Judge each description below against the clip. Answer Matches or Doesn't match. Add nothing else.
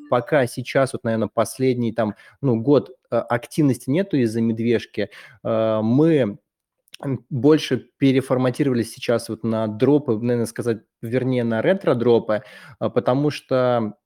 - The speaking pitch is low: Matches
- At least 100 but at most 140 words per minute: Matches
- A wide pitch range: Doesn't match